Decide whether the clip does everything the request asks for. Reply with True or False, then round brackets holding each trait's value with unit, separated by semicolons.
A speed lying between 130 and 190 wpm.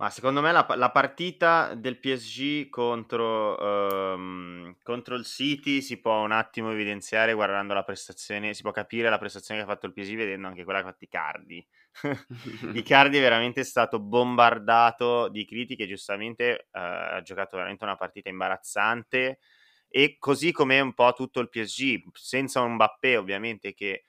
True (160 wpm)